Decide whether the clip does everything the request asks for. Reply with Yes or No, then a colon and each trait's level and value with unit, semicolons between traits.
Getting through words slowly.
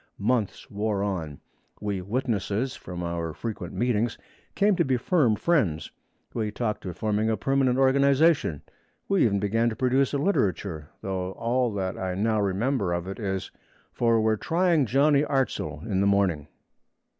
No: average, 155 wpm